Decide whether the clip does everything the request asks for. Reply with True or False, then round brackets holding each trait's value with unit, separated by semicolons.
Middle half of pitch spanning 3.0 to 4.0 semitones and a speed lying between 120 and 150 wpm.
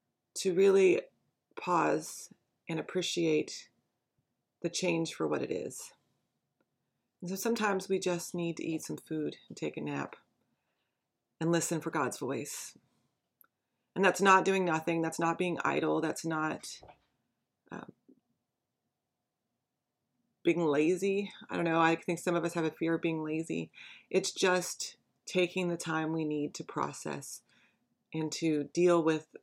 False (2.5 semitones; 145 wpm)